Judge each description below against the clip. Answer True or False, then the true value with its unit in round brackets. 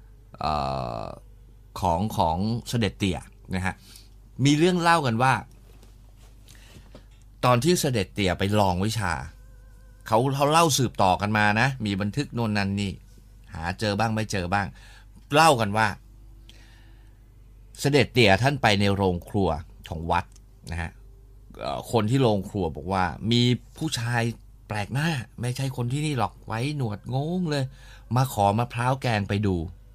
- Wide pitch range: False (3.2 semitones)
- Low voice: True (110 Hz)